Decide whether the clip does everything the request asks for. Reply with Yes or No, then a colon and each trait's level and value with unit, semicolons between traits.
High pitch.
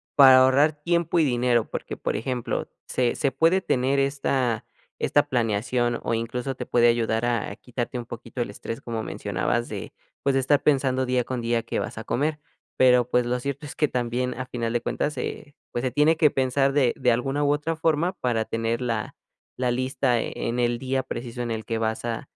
No: low, 125 Hz